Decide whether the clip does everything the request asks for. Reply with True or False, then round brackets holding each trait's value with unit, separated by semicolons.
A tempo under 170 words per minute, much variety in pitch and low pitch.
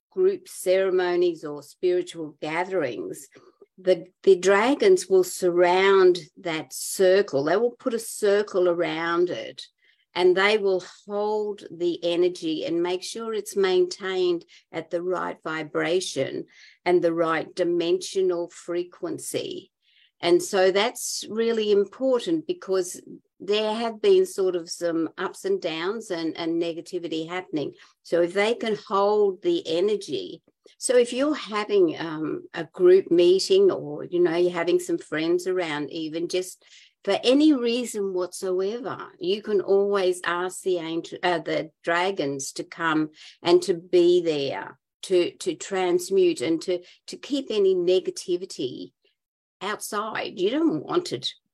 False (135 wpm; 8.8 semitones; 190 Hz)